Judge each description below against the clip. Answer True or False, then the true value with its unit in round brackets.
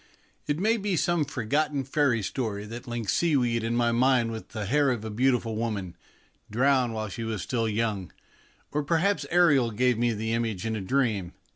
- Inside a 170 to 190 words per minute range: True (185 wpm)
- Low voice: True (120 Hz)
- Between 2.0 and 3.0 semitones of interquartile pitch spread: False (3.9 semitones)